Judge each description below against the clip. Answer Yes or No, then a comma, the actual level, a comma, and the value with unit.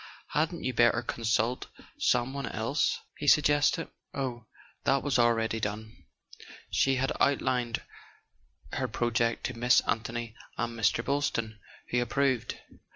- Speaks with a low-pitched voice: Yes, low, 120 Hz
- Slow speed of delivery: Yes, slow, 130 wpm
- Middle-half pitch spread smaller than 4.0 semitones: Yes, average, 2.8 semitones